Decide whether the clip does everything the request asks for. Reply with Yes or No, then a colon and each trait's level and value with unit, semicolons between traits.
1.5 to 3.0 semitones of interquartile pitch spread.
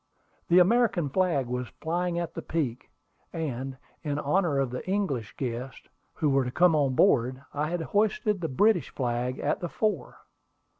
No: wide, 5.6 semitones